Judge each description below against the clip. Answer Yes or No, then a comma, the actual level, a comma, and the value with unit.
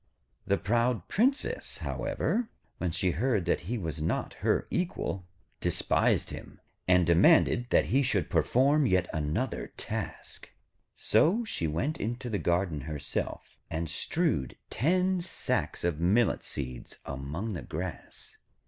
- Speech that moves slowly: Yes, slow, 130 wpm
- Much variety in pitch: Yes, wide, 8.0 semitones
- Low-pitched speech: Yes, very low, 95 Hz